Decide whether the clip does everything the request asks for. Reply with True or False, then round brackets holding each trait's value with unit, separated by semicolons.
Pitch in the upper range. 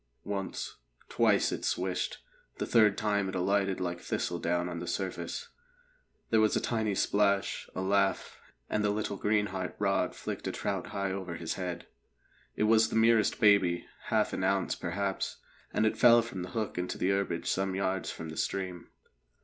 False (95 Hz)